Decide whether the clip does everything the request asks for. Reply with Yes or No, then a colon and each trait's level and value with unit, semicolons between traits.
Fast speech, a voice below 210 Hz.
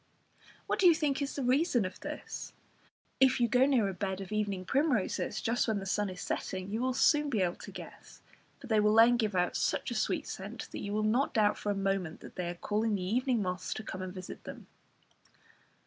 No: fast, 230 wpm; high, 215 Hz